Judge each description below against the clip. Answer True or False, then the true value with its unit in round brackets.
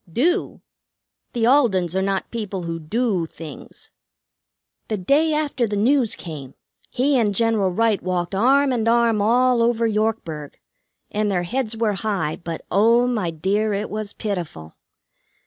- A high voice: True (215 Hz)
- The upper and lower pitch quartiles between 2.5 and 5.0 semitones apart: True (4.3 semitones)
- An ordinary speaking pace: True (145 wpm)